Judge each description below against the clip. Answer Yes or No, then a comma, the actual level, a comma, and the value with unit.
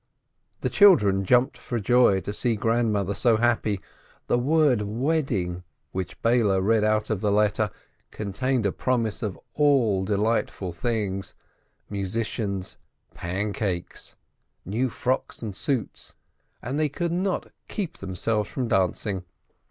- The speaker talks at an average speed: No, slow, 125 wpm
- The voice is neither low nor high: No, low, 110 Hz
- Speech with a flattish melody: No, average, 3.9 semitones